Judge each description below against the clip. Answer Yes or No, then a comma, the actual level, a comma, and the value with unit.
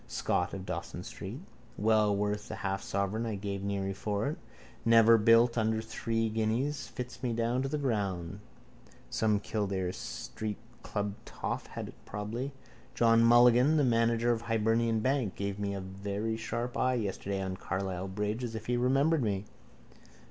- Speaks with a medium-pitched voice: No, low, 110 Hz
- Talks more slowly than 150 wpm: No, average, 165 wpm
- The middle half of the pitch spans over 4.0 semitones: No, average, 2.9 semitones